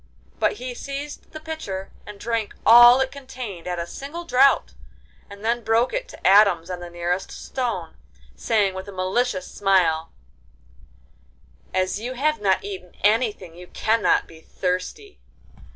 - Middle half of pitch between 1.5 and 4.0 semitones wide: No, wide, 5.5 semitones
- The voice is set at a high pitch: Yes, high, 210 Hz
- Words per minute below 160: Yes, average, 150 wpm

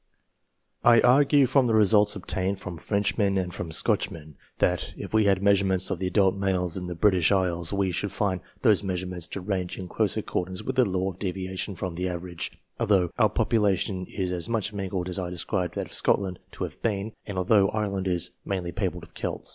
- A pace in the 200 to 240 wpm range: Yes, fast, 205 wpm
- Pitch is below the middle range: Yes, very low, 95 Hz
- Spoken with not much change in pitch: Yes, narrow, 2.2 semitones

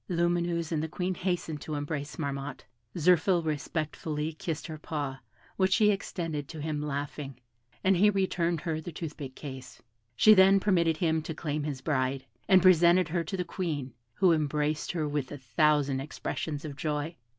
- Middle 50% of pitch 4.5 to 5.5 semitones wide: No, average, 3.0 semitones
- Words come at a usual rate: Yes, average, 170 wpm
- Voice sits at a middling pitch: Yes, medium, 155 Hz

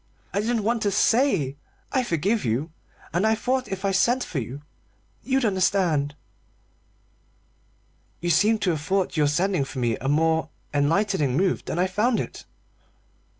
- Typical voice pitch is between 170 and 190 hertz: Yes, medium, 185 Hz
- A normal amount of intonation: No, wide, 6.5 semitones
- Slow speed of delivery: No, average, 155 wpm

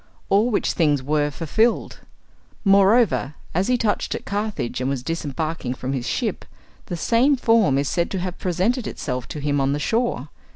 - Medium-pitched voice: Yes, medium, 170 Hz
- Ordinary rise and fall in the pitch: No, wide, 7.2 semitones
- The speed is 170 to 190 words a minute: Yes, average, 175 wpm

